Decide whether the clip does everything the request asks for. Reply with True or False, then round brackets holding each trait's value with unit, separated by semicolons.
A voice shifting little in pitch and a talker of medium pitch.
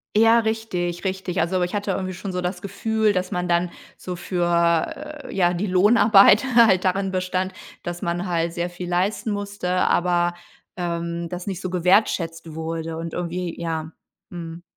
True (2.0 semitones; 180 Hz)